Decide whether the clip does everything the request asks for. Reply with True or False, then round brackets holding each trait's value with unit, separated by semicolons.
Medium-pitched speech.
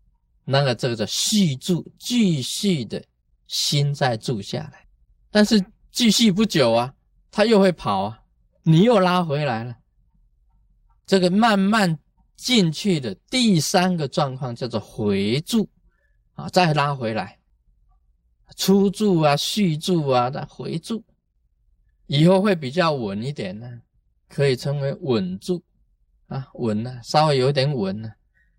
True (155 Hz)